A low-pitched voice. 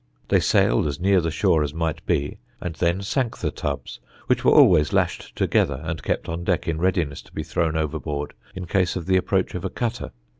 Yes: very low, 80 Hz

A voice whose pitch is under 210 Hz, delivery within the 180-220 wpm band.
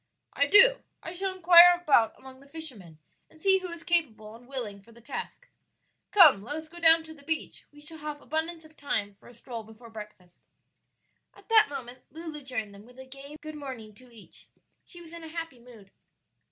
No: very high, 285 Hz; fast, 205 wpm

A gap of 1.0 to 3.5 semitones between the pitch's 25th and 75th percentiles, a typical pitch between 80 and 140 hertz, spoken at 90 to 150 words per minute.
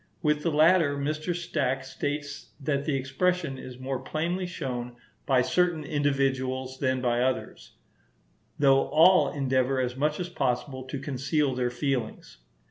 Yes: average, 2.8 semitones; low, 135 Hz; average, 140 wpm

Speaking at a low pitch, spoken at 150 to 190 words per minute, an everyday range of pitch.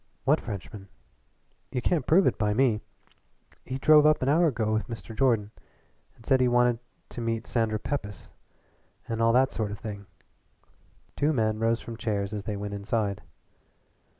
Yes: low, 115 Hz; average, 170 wpm; average, 3.5 semitones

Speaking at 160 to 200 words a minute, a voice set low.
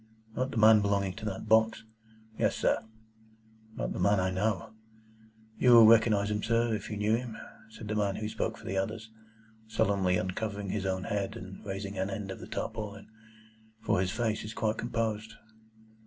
Yes: average, 185 wpm; low, 105 Hz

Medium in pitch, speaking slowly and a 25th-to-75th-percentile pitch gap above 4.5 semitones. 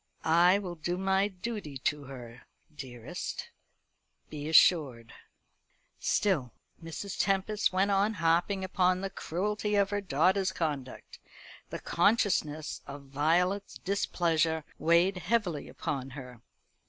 Yes: medium, 175 Hz; slow, 115 wpm; average, 5.0 semitones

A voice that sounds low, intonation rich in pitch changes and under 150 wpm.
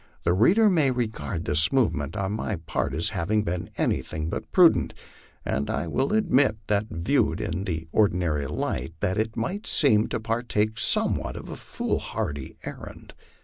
No: low, 105 Hz; wide, 6.3 semitones; average, 155 wpm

